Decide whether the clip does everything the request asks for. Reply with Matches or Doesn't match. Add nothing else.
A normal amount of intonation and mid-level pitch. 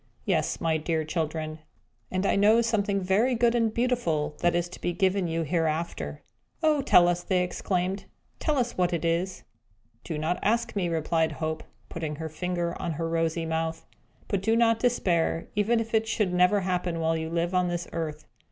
Matches